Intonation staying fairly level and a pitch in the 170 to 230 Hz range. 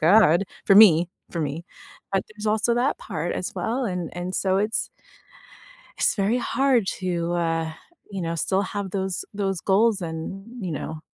No: average, 3.9 semitones; high, 190 Hz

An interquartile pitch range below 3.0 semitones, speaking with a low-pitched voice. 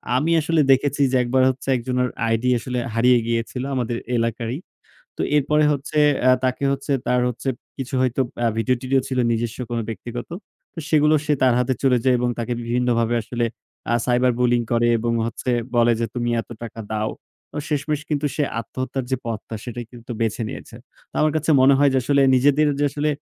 Yes: narrow, 2.6 semitones; low, 125 Hz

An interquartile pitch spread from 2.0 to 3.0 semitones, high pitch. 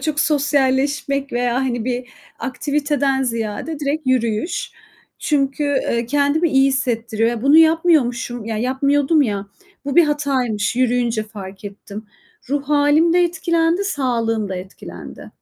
No: average, 3.9 semitones; very high, 265 Hz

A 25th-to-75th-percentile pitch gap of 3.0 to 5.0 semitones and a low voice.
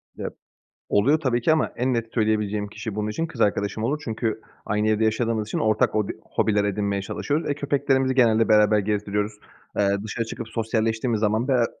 No: narrow, 2.5 semitones; low, 110 Hz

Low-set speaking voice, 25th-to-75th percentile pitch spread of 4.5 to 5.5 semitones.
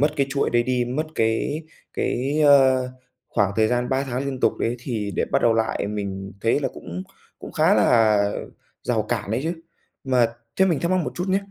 No: low, 125 Hz; average, 4.0 semitones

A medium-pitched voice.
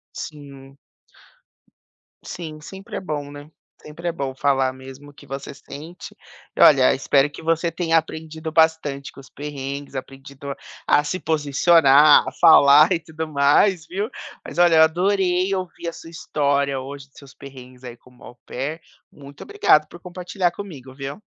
Yes: medium, 150 Hz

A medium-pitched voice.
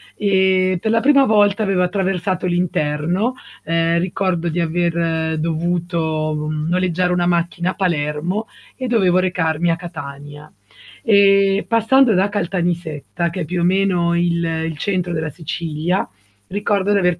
Yes: medium, 175 Hz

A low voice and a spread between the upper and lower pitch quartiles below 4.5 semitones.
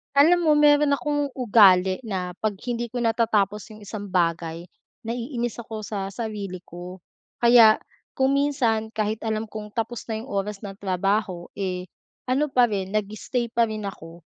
No: high, 215 Hz; average, 3.5 semitones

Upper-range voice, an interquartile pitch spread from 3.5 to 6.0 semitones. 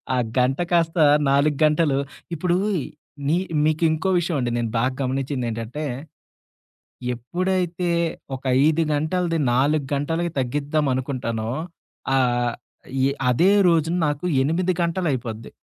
No: medium, 150 Hz; average, 4.6 semitones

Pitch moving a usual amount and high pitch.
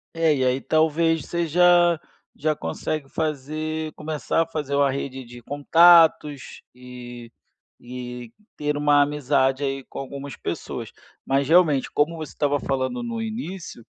No: average, 3.3 semitones; medium, 145 Hz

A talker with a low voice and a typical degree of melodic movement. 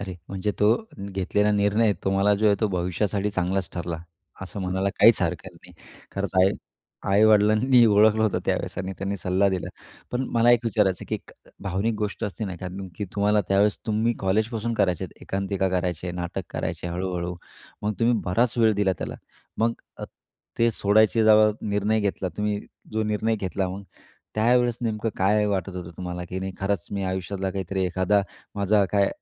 No: low, 100 Hz; narrow, 2.3 semitones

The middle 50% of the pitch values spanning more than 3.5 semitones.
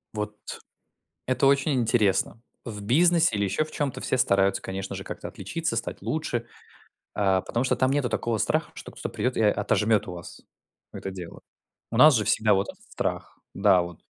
Yes: average, 4.9 semitones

